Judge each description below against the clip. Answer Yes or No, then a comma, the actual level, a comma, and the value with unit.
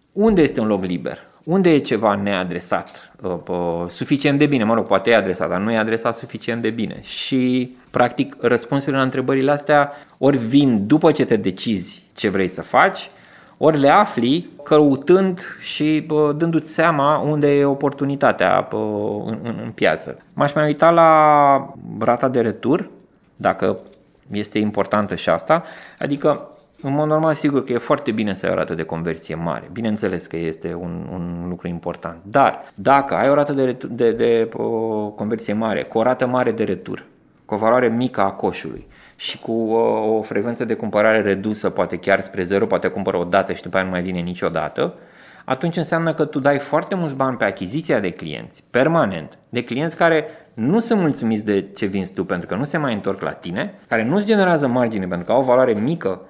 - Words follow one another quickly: Yes, fast, 185 wpm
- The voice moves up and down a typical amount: No, wide, 6.1 semitones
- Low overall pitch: Yes, low, 125 Hz